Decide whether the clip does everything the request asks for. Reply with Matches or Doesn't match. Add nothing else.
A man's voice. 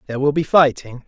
Matches